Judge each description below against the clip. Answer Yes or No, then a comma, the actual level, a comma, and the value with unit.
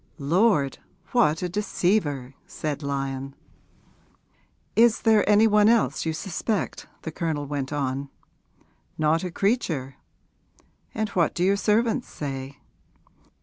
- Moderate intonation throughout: No, wide, 6.9 semitones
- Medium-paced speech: No, slow, 115 wpm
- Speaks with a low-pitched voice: No, medium, 165 Hz